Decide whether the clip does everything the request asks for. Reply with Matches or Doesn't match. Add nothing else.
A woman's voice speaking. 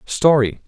Doesn't match